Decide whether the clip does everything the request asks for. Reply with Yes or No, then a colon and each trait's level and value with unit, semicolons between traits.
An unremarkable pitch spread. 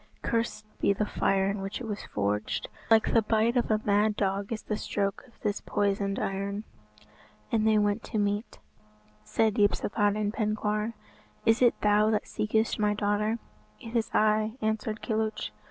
No: narrow, 1.3 semitones